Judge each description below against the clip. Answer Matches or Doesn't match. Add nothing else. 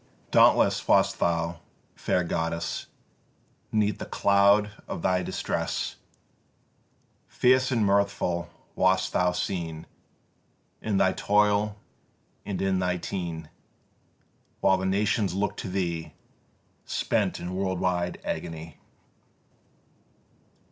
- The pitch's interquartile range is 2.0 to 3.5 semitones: Matches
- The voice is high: Doesn't match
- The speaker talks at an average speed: Doesn't match